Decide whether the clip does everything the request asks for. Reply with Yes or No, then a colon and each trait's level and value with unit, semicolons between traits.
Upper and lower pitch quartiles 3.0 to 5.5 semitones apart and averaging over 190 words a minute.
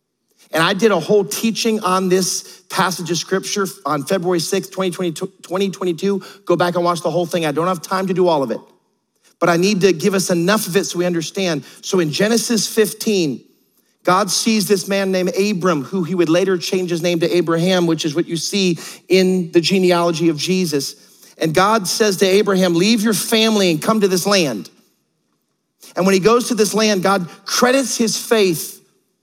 No: narrow, 2.4 semitones; average, 200 wpm